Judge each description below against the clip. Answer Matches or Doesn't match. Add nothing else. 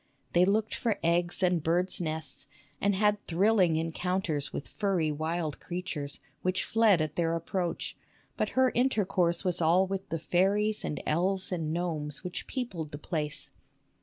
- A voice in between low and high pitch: Matches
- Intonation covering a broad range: Doesn't match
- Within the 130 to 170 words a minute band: Matches